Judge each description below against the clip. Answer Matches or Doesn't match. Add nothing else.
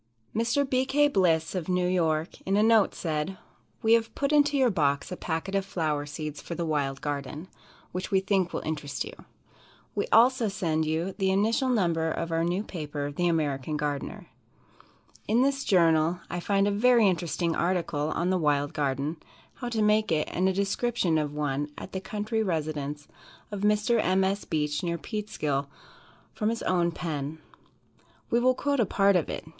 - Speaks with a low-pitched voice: Doesn't match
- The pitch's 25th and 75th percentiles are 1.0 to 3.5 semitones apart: Doesn't match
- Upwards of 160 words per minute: Matches